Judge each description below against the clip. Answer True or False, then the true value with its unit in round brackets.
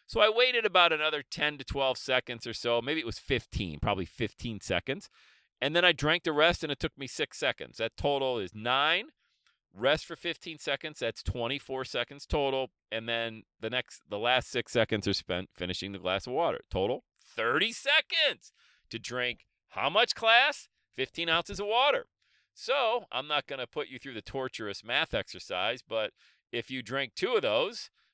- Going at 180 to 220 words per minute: True (190 wpm)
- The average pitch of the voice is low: True (130 Hz)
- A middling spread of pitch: False (6.6 semitones)